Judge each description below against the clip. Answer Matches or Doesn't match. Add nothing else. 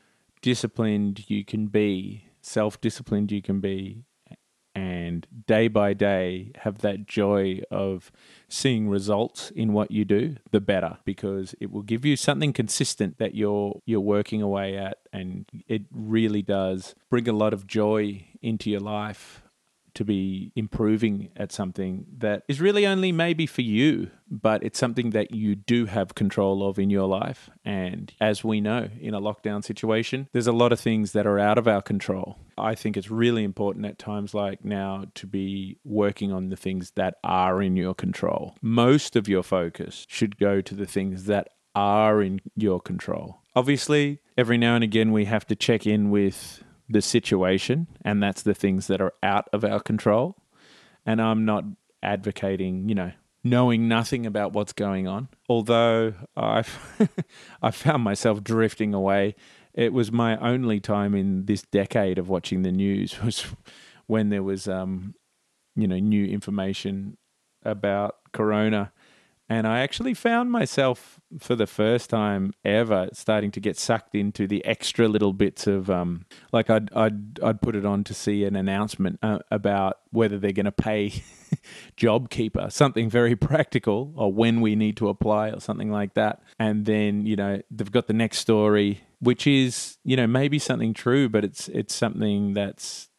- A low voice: Matches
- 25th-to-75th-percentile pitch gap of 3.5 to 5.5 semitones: Doesn't match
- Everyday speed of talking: Matches